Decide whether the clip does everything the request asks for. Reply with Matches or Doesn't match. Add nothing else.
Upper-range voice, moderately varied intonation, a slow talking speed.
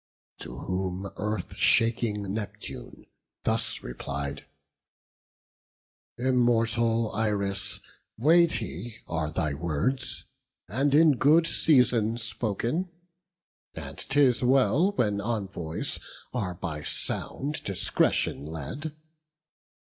Doesn't match